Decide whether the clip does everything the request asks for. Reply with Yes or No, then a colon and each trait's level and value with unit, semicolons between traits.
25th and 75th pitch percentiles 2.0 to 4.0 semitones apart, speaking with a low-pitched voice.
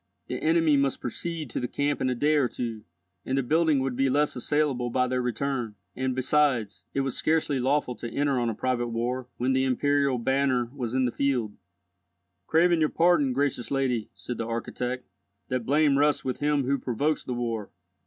Yes: average, 2.8 semitones; low, 130 Hz